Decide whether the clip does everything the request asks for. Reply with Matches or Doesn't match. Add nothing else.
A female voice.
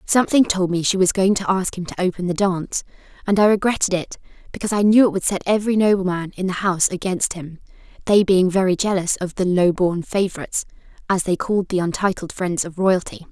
Matches